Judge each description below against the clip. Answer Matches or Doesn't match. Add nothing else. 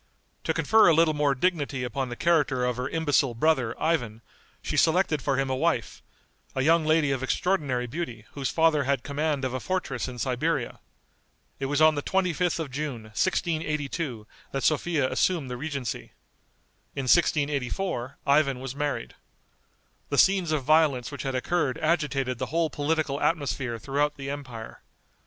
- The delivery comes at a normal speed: Matches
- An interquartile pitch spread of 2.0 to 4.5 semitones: Matches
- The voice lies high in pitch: Doesn't match